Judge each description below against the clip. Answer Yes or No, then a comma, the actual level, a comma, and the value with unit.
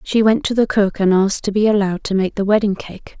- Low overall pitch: No, high, 205 Hz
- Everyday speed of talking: No, fast, 280 wpm